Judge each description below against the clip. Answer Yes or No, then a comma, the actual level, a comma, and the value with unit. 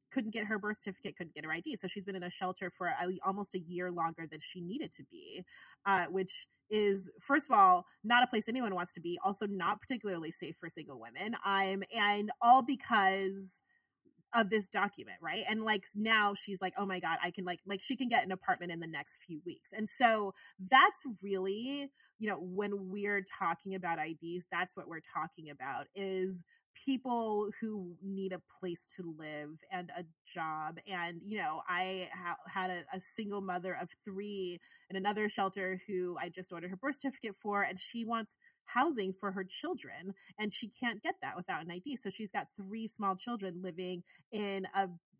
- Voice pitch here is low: No, high, 195 Hz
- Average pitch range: Yes, average, 3.3 semitones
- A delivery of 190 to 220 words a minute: Yes, average, 200 wpm